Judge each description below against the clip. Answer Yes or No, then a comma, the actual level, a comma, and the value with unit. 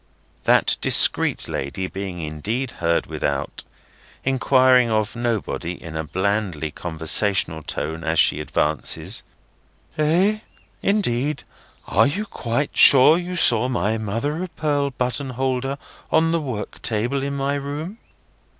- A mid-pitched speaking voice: No, low, 120 Hz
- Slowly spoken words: Yes, slow, 125 wpm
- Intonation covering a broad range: Yes, wide, 7.3 semitones